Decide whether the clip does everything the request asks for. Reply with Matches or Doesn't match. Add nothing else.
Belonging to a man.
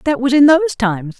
Doesn't match